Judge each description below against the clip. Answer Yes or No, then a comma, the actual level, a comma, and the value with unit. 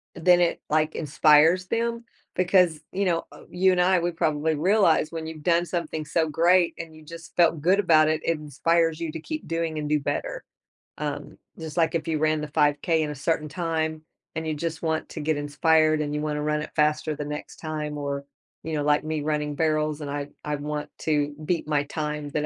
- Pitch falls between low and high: Yes, medium, 155 Hz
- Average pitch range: No, narrow, 1.8 semitones